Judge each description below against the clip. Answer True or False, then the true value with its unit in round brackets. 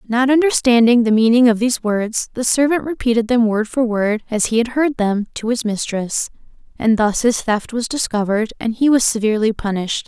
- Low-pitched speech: False (230 Hz)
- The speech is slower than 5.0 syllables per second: False (5.4 syllables/s)